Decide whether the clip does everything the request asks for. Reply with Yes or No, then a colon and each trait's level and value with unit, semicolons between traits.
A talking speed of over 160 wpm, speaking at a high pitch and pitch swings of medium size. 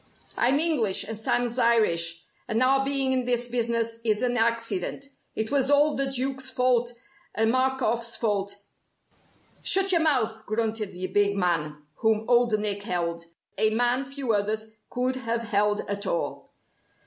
No: average, 155 wpm; high, 230 Hz; average, 3.5 semitones